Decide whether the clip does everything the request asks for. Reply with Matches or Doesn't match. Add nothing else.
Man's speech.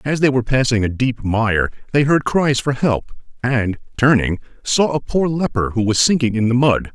Matches